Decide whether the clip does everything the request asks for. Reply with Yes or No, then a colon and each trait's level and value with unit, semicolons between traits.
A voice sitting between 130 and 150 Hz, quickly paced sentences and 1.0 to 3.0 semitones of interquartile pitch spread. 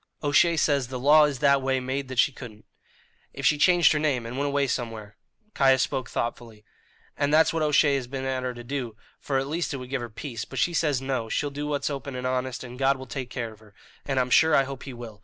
Yes: low, 135 Hz; fast, 260 wpm; average, 2.7 semitones